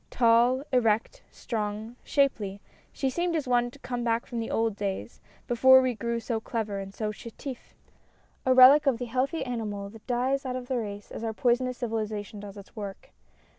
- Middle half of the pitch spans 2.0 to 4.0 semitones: Yes, average, 3.1 semitones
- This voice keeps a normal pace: Yes, average, 185 wpm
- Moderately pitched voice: No, high, 235 Hz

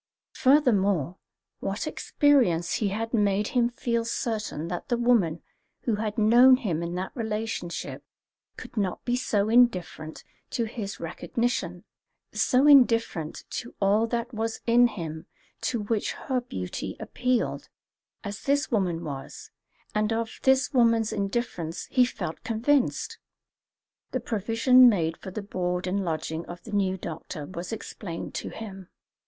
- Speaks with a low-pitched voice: No, high, 215 Hz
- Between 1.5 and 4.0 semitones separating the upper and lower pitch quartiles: No, average, 5.0 semitones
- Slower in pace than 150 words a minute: Yes, average, 140 wpm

